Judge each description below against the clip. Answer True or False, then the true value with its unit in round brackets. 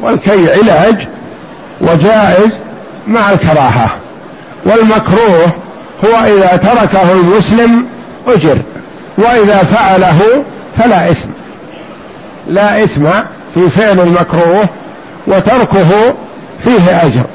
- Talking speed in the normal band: True (80 wpm)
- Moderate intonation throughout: True (3.8 semitones)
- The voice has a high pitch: True (195 Hz)